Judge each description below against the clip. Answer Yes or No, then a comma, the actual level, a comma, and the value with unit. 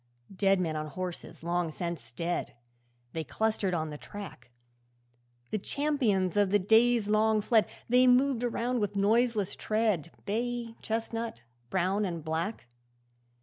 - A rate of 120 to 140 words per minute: Yes, slow, 135 wpm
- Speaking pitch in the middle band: No, high, 205 Hz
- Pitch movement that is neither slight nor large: Yes, average, 4.5 semitones